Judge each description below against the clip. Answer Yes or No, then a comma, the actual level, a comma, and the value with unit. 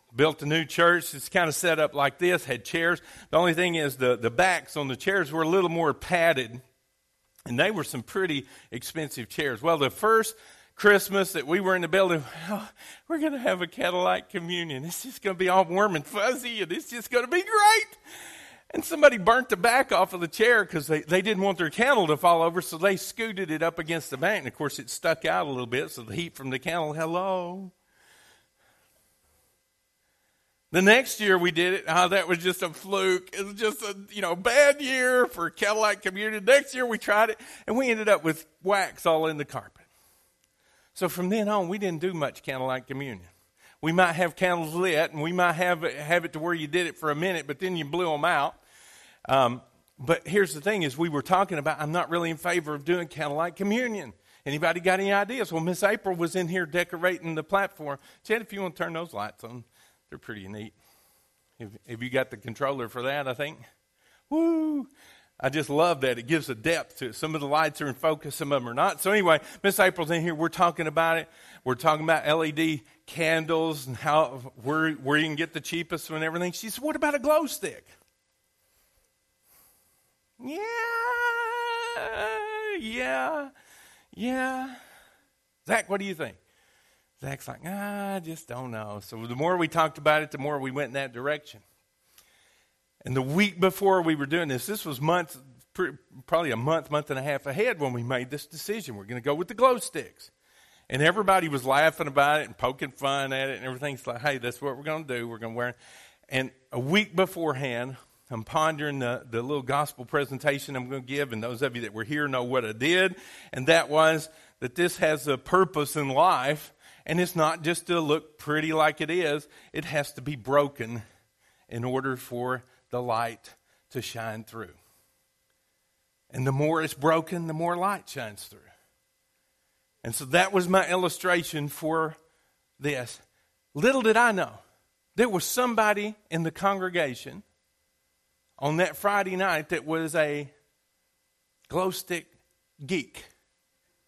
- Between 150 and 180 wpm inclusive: No, average, 200 wpm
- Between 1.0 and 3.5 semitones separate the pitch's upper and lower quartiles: No, wide, 5.5 semitones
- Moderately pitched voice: Yes, medium, 160 Hz